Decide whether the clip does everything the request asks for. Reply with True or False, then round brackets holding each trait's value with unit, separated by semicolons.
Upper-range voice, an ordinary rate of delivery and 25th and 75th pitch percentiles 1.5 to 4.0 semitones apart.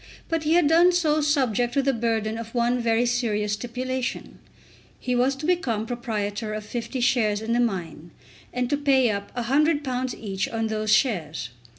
True (240 Hz; 175 wpm; 3.7 semitones)